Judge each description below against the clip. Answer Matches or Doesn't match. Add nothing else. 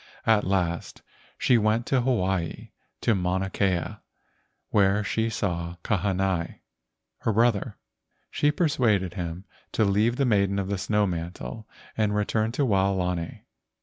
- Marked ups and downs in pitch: Doesn't match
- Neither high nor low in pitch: Doesn't match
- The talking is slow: Matches